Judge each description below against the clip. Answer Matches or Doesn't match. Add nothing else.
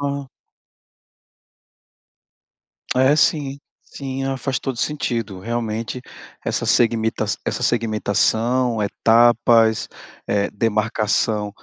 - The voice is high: Doesn't match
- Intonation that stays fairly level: Doesn't match